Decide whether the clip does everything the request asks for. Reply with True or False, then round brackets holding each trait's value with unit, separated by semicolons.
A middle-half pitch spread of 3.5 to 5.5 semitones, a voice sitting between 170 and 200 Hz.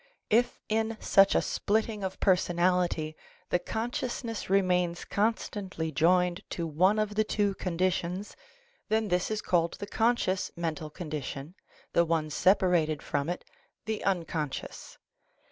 True (3.8 semitones; 185 Hz)